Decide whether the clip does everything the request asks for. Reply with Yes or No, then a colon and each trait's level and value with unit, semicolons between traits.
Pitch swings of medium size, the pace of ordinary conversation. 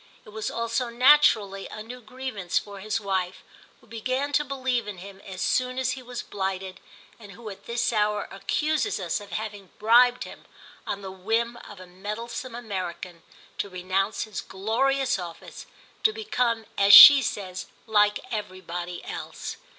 Yes: average, 4.2 semitones; average, 160 wpm